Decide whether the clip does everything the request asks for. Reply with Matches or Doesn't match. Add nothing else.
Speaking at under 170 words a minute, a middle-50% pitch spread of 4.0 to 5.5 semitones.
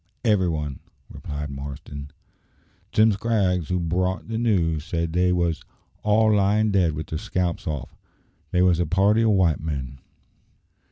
Matches